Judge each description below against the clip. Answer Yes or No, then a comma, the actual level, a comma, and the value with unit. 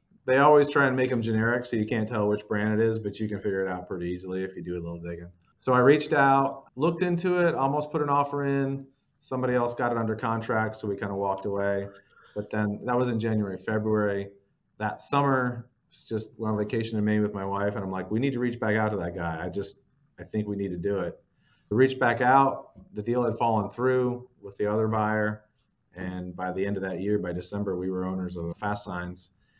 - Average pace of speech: No, fast, 245 wpm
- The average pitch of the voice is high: No, low, 110 Hz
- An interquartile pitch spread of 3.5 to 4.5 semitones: Yes, average, 4.0 semitones